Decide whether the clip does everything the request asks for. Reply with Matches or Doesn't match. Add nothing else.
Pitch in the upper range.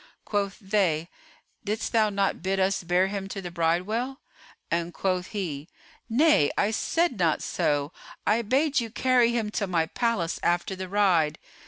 Matches